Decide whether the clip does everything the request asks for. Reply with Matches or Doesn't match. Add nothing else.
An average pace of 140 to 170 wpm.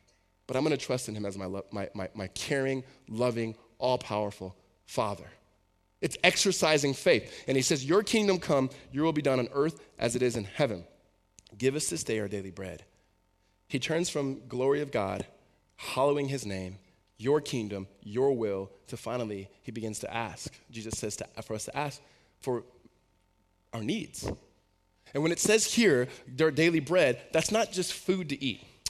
Doesn't match